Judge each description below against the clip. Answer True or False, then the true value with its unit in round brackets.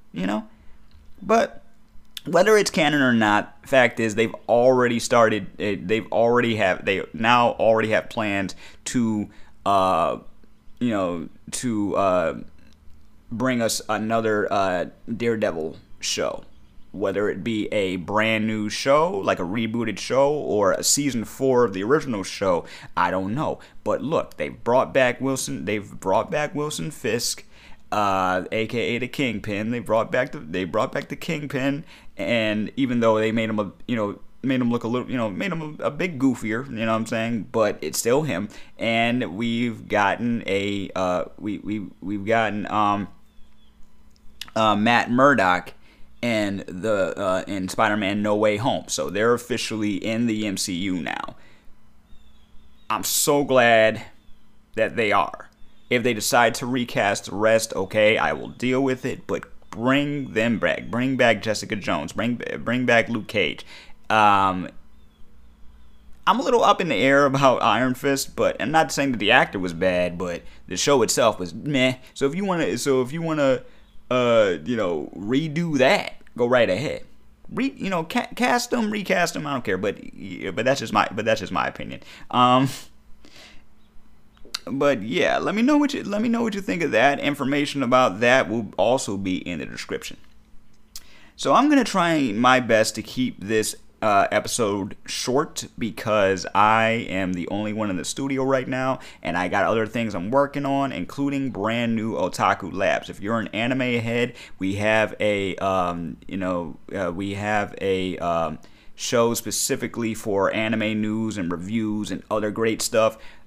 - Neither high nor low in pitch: False (115 Hz)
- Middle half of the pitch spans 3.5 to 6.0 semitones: True (3.8 semitones)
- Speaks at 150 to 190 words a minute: True (170 wpm)